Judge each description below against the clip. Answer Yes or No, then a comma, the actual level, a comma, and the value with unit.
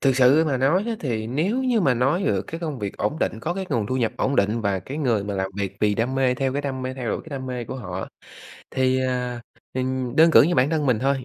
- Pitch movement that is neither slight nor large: Yes, average, 3.8 semitones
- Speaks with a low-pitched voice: Yes, low, 130 Hz